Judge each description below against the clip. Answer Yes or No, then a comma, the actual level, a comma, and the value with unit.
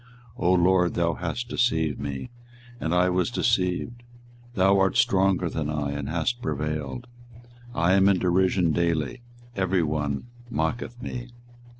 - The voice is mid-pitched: No, very low, 90 Hz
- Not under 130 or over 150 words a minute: Yes, average, 140 wpm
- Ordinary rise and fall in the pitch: Yes, average, 3.5 semitones